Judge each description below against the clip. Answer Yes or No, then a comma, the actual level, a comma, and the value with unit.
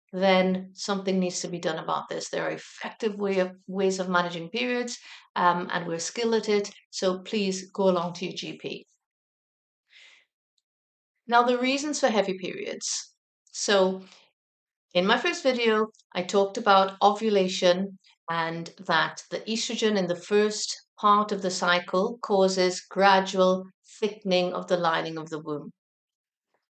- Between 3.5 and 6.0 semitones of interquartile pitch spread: No, average, 3.1 semitones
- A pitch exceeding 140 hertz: Yes, high, 190 Hz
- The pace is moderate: Yes, average, 145 wpm